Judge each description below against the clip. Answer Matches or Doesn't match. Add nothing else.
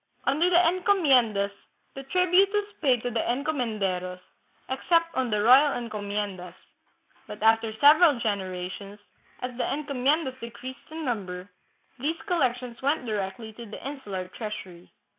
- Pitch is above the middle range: Matches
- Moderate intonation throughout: Doesn't match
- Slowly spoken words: Matches